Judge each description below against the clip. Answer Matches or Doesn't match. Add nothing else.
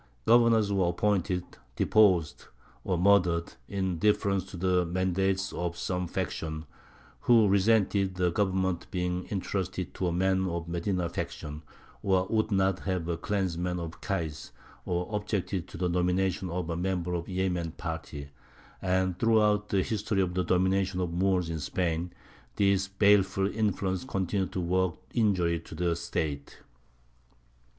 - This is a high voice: Doesn't match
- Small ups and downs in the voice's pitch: Matches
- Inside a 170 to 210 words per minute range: Doesn't match